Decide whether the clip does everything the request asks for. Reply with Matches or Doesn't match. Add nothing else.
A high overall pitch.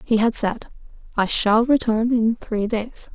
Matches